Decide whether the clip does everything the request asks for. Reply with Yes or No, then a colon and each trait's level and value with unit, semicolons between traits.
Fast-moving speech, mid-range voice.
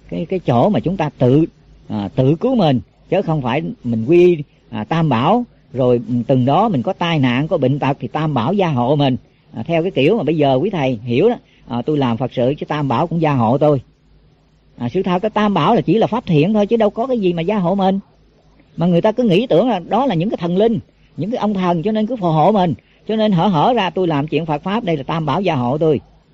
Yes: fast, 270 wpm; medium, 160 Hz